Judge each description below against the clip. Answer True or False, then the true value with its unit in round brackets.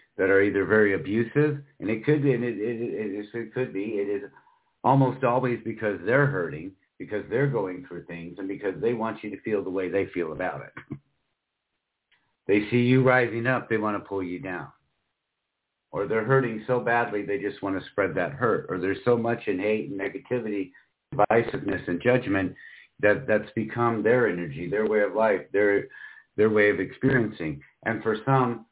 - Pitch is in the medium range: False (110 Hz)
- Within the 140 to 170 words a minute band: False (195 wpm)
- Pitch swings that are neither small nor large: True (3.7 semitones)